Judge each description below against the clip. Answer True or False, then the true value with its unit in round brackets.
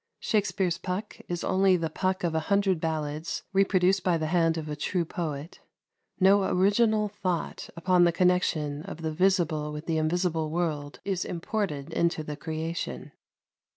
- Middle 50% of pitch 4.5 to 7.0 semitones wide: False (3.1 semitones)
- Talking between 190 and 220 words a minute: False (155 wpm)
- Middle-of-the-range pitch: True (170 Hz)